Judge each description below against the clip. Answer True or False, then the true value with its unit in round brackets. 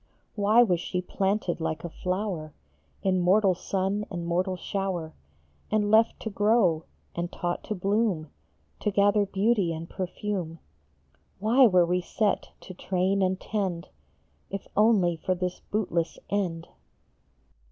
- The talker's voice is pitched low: False (190 Hz)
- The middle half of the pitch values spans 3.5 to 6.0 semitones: False (2.9 semitones)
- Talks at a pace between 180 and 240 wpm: False (135 wpm)